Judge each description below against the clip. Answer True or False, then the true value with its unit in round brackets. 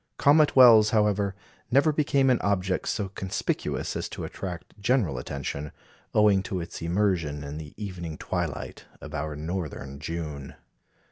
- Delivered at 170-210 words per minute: False (140 wpm)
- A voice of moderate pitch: False (95 Hz)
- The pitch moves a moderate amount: False (5.7 semitones)